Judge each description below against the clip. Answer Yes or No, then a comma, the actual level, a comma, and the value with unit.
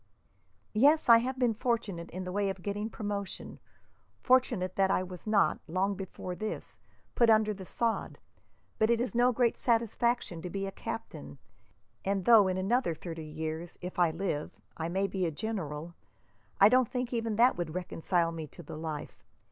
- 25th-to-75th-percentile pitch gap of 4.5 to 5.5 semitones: Yes, average, 4.8 semitones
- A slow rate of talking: No, average, 180 wpm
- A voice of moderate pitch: No, high, 195 Hz